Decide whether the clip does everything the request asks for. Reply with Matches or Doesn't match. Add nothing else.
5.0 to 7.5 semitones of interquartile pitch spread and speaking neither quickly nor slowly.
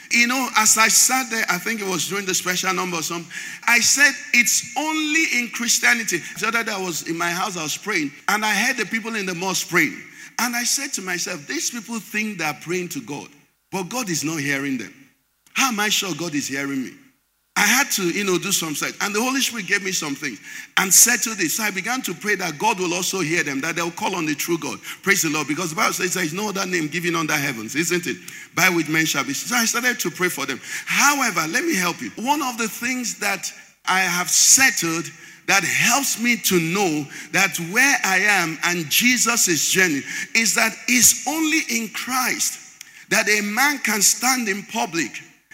Doesn't match